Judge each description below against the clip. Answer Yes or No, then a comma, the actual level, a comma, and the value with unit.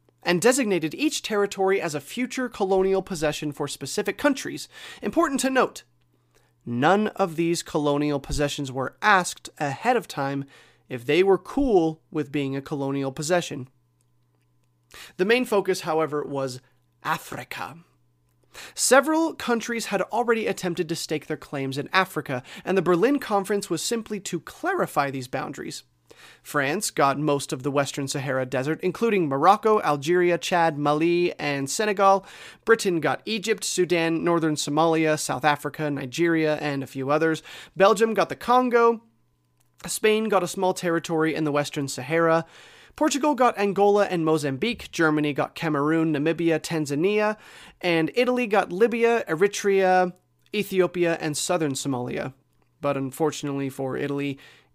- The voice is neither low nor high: Yes, medium, 165 Hz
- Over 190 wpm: No, slow, 135 wpm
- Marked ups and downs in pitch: Yes, wide, 5.8 semitones